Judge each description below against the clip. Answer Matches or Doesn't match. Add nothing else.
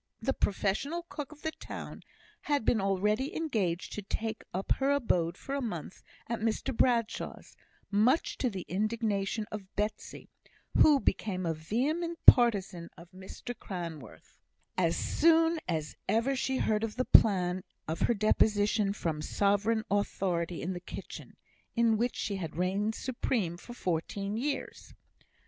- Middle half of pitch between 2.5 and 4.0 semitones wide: Doesn't match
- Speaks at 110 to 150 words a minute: Matches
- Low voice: Doesn't match